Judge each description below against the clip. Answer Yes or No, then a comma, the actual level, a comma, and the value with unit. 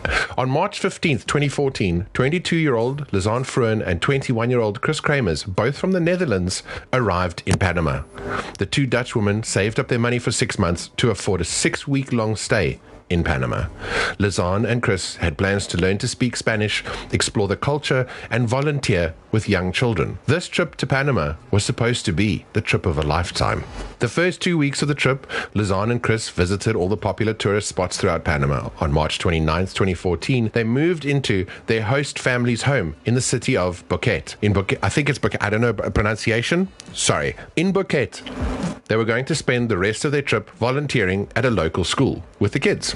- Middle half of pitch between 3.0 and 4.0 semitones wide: No, wide, 5.5 semitones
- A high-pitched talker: No, low, 115 Hz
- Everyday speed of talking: Yes, average, 185 wpm